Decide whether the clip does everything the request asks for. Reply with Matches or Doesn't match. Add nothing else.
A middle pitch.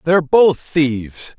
Matches